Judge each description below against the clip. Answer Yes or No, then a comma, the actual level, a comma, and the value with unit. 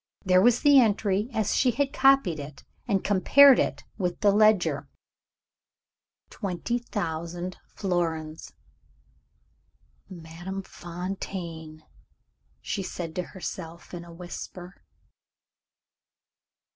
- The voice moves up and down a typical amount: Yes, average, 3.9 semitones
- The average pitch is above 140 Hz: Yes, medium, 185 Hz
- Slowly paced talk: Yes, slow, 95 wpm